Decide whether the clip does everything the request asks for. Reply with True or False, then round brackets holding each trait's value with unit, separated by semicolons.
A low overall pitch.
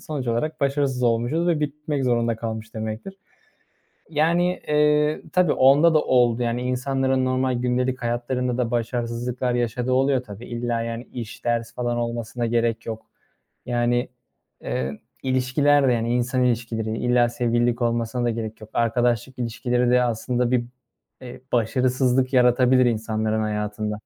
True (120 Hz)